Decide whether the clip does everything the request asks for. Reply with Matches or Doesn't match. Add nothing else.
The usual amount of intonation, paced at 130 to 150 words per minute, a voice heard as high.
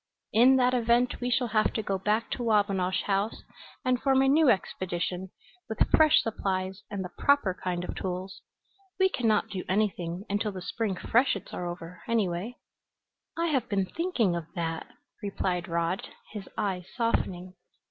Doesn't match